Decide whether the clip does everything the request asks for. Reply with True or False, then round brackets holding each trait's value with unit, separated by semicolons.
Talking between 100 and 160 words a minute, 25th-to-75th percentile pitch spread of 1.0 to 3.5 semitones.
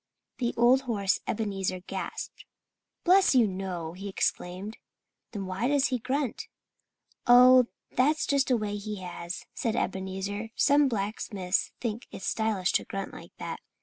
False (145 wpm; 4.7 semitones)